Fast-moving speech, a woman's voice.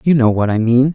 No: fast, 320 wpm; male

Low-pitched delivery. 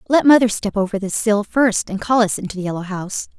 No: high, 210 Hz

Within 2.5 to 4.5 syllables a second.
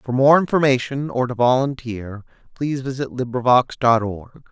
No: 4.9 syllables/s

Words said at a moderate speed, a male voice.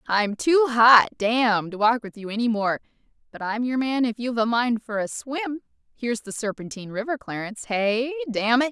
No: average, 180 wpm; female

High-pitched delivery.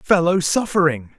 No: medium, 170 Hz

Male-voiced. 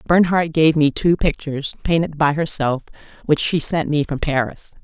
No: female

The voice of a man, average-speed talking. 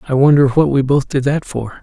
No: male; fast, 265 wpm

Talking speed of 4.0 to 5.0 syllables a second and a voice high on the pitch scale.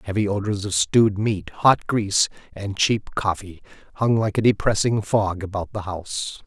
No: 4.8 syllables/s; low, 100 Hz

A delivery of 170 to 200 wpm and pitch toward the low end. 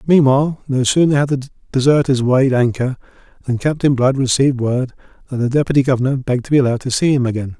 Yes: average, 195 wpm; low, 130 Hz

